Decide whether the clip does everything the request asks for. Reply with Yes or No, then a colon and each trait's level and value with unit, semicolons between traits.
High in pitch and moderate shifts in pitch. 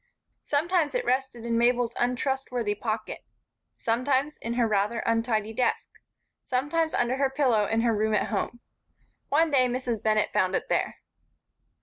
Yes: high, 240 Hz; average, 3.1 semitones